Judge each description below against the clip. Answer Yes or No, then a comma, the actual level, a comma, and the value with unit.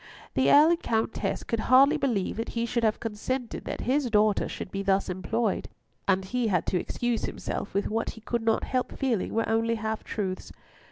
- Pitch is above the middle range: Yes, high, 225 Hz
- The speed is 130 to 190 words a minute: No, average, 200 wpm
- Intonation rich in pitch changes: No, average, 3.3 semitones